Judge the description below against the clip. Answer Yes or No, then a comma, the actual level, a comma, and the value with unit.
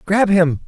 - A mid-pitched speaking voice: Yes, medium, 180 Hz